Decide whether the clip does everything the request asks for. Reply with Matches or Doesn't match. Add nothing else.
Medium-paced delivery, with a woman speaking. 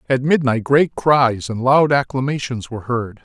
Doesn't match